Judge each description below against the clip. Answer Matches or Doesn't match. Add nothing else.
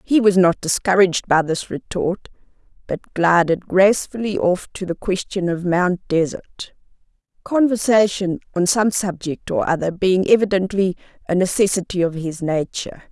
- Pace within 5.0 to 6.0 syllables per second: Doesn't match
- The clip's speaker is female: Matches